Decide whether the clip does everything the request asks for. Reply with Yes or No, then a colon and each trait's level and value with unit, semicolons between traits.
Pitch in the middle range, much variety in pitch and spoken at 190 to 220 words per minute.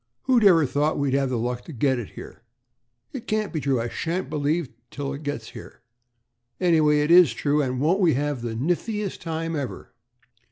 No: medium, 150 Hz; average, 4.2 semitones; average, 195 wpm